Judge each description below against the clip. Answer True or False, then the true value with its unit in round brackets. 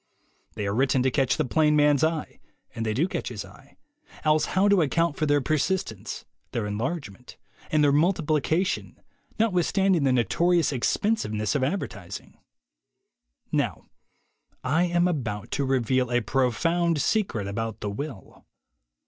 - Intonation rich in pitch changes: True (6.0 semitones)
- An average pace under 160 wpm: True (145 wpm)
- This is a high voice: False (145 Hz)